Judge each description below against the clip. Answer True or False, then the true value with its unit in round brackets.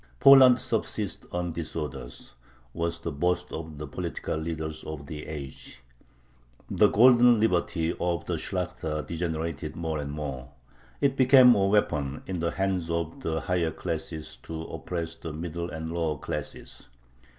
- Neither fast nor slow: True (150 wpm)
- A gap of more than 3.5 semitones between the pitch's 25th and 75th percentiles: False (2.5 semitones)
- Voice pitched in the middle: False (80 Hz)